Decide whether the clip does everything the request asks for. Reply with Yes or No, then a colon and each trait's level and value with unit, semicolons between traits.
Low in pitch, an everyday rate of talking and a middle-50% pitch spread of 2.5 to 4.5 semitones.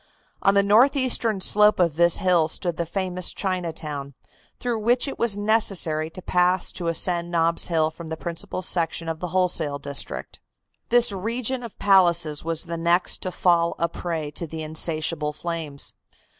No: medium, 175 Hz; average, 165 wpm; average, 3.3 semitones